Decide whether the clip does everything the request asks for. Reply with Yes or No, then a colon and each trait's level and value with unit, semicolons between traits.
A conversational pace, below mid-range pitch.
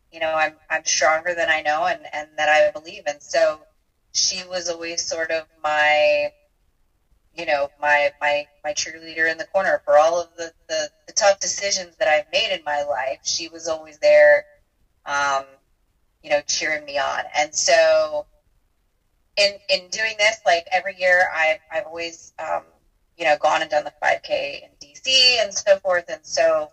No: average, 185 wpm; medium, 160 Hz